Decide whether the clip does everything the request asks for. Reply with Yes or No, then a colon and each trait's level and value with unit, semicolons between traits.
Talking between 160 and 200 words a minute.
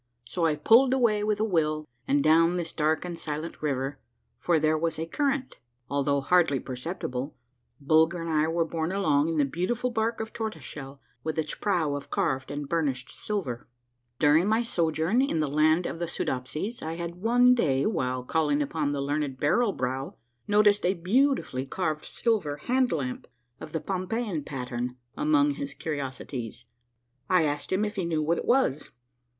Yes: average, 180 wpm